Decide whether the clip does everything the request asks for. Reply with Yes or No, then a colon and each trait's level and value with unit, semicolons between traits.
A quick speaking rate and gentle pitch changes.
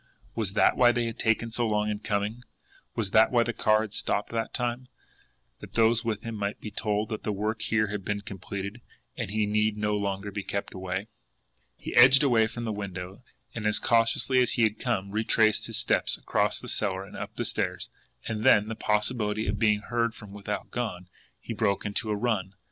Yes: fast, 210 wpm; narrow, 2.0 semitones